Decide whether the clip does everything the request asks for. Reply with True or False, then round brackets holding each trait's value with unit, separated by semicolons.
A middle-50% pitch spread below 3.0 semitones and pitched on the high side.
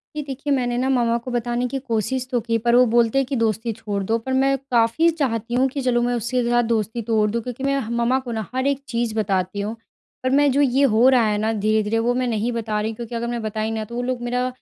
True (2.5 semitones; 240 Hz)